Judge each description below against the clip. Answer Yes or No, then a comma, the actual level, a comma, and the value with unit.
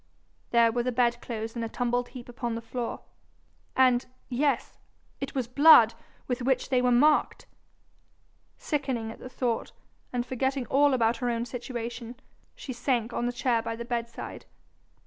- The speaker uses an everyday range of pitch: No, narrow, 1.7 semitones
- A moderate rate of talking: Yes, average, 160 wpm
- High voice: Yes, high, 245 Hz